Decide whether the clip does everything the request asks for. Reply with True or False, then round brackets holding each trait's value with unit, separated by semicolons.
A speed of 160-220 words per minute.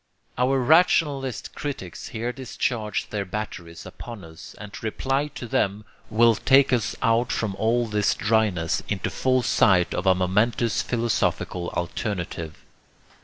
False (135 wpm)